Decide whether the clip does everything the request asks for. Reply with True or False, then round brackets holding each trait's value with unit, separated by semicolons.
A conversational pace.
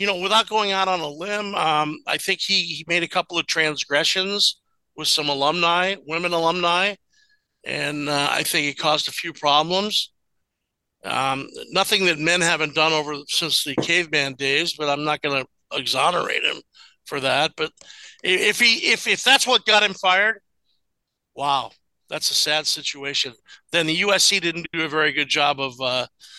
True (175 wpm)